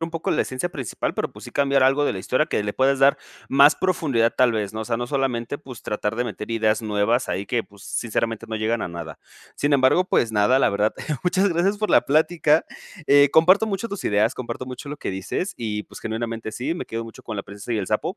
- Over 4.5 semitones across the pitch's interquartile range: Yes, average, 4.9 semitones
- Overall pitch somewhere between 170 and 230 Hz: No, low, 120 Hz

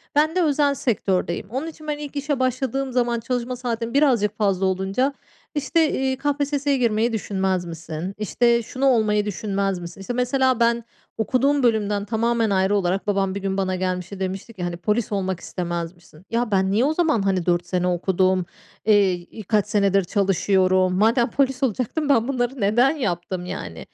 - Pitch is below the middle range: No, high, 210 Hz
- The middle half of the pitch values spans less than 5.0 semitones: No, average, 5.3 semitones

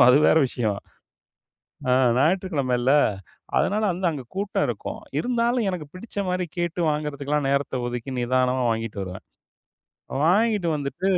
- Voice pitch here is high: No, medium, 150 Hz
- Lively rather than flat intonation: Yes, wide, 6.6 semitones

